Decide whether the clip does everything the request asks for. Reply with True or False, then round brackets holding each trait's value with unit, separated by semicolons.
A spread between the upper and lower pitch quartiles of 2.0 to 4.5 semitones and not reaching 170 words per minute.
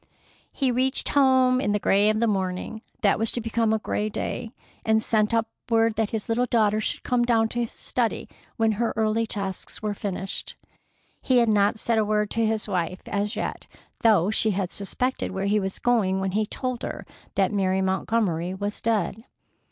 False (2.4 semitones; 195 wpm)